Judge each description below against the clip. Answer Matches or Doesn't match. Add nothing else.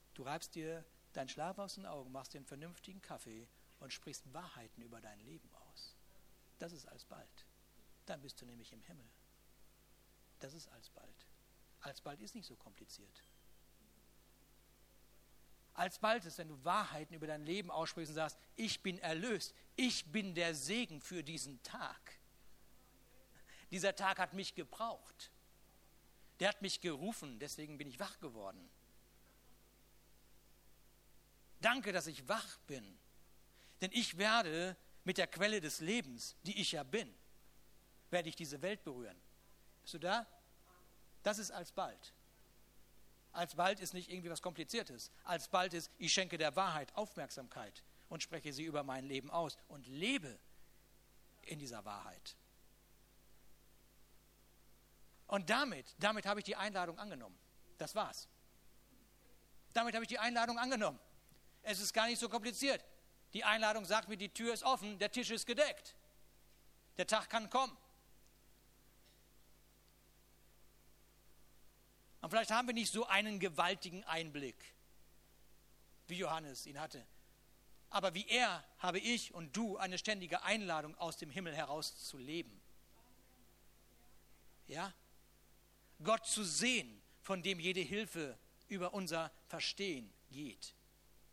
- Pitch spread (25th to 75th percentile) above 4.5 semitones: Matches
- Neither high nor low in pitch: Matches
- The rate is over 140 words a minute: Doesn't match